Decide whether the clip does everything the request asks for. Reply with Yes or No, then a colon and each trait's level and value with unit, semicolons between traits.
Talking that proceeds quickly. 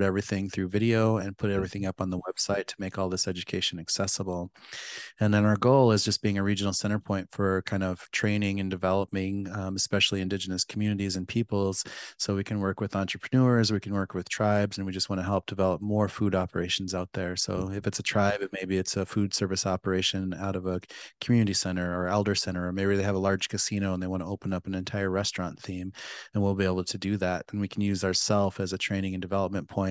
Yes: fast, 235 wpm